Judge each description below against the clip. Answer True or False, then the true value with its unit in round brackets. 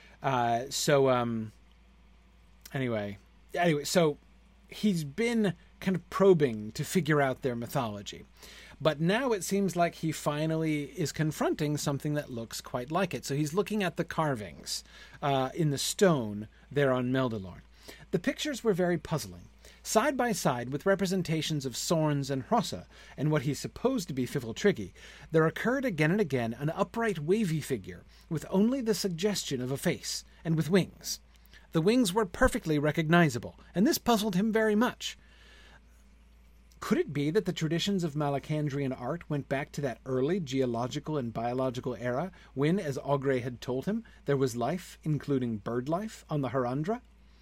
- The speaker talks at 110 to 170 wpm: True (160 wpm)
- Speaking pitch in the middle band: True (150 Hz)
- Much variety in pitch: True (6.3 semitones)